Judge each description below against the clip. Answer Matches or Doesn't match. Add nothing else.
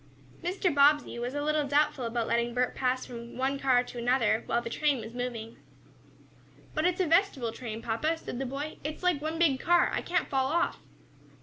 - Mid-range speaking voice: Doesn't match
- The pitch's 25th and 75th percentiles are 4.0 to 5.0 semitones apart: Matches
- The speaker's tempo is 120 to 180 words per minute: Doesn't match